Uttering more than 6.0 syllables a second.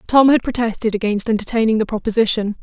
Yes: 6.5 syllables/s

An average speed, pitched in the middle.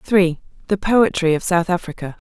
Yes: average, 160 wpm; medium, 180 Hz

